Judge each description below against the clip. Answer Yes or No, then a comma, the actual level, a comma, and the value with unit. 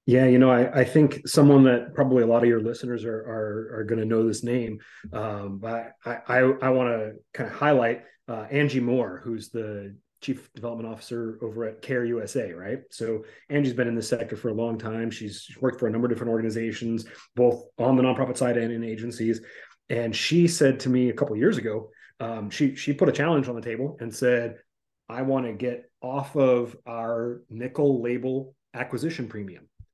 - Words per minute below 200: No, fast, 205 wpm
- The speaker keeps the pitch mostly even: Yes, narrow, 2.3 semitones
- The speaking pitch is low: Yes, low, 120 Hz